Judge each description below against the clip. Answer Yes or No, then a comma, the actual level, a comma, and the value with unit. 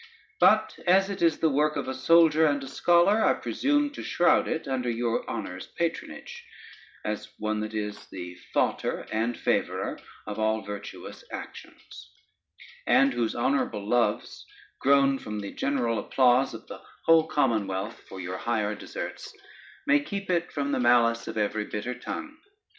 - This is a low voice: Yes, low, 125 Hz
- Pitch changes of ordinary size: No, wide, 7.3 semitones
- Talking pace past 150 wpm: Yes, average, 160 wpm